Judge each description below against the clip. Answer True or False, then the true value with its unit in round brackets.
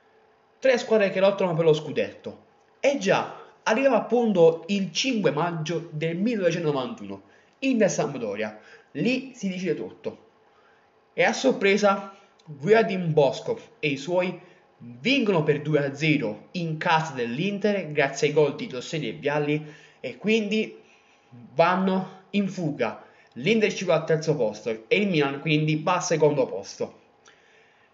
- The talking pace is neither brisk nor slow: True (135 wpm)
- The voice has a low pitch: False (180 Hz)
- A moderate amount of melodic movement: False (6.0 semitones)